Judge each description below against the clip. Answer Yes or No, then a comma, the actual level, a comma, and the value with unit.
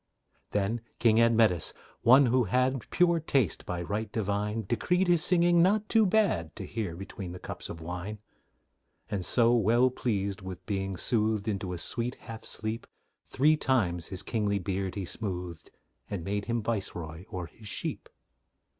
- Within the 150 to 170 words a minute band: Yes, average, 160 wpm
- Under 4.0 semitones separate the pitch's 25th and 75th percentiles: No, average, 4.6 semitones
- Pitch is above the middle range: No, low, 110 Hz